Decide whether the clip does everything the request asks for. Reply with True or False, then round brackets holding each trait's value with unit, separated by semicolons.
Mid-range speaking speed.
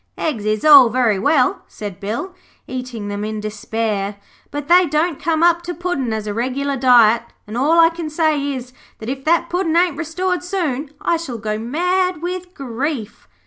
True (185 wpm)